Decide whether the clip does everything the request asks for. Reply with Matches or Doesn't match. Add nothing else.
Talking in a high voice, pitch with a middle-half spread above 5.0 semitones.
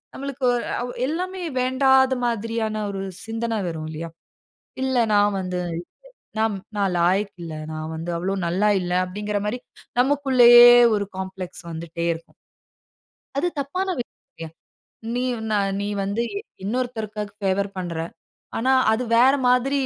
Matches